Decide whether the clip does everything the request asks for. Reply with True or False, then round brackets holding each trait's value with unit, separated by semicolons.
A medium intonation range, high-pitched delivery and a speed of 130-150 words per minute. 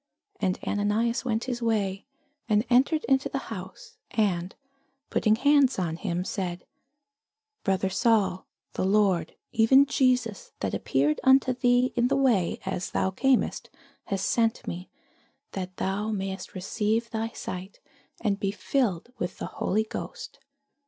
True (4.4 semitones; 210 Hz; 140 wpm)